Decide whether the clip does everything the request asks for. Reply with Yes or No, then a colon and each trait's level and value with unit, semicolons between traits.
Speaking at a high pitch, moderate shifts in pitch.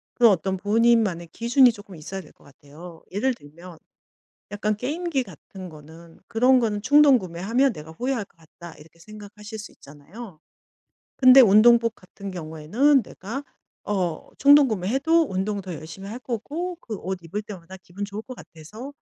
No: high, 205 Hz; wide, 5.9 semitones